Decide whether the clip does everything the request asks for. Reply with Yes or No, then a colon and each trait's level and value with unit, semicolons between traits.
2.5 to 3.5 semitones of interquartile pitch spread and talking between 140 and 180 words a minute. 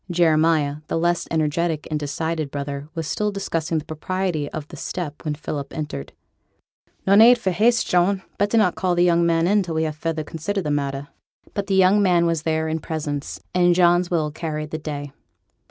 No: average, 2.9 semitones; average, 190 wpm